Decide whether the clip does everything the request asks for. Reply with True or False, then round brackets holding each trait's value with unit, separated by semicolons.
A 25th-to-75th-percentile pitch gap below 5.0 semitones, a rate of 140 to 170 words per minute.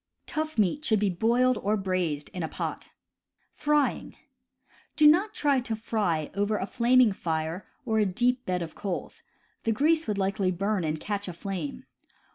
False (5.5 semitones; 160 wpm)